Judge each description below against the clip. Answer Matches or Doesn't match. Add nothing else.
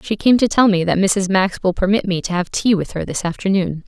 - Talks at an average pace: Doesn't match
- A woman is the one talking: Matches